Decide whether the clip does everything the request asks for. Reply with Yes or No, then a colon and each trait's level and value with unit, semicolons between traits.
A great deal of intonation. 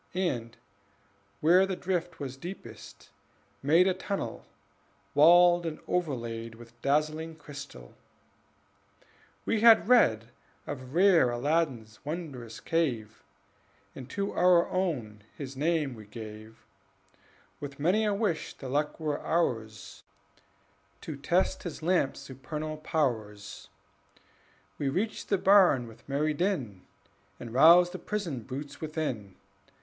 Yes: wide, 6.4 semitones